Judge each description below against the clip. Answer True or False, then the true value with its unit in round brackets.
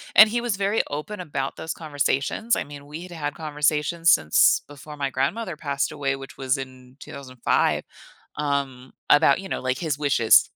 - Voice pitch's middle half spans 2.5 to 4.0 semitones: True (3.4 semitones)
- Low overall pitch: False (145 Hz)